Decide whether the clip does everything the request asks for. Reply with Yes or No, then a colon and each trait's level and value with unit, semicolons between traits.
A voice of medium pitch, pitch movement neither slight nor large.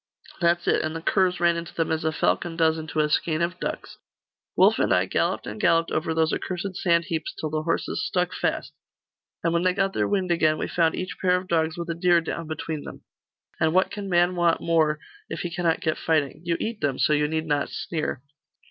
No: medium, 165 Hz; narrow, 1.8 semitones